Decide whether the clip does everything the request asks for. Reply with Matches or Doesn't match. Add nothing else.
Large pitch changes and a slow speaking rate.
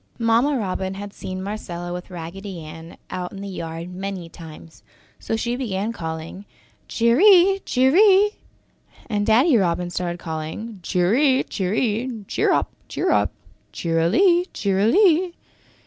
Matches